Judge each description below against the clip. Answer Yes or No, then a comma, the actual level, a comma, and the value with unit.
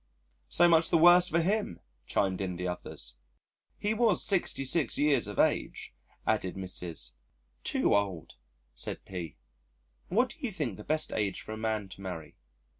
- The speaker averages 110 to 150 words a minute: No, average, 160 wpm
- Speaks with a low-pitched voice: Yes, low, 110 Hz